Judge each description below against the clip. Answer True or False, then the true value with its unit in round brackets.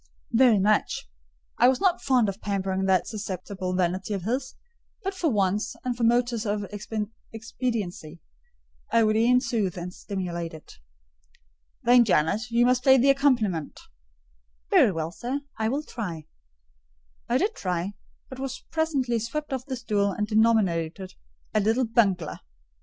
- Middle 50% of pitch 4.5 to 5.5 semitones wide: True (4.9 semitones)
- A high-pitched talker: True (220 Hz)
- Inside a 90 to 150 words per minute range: True (145 wpm)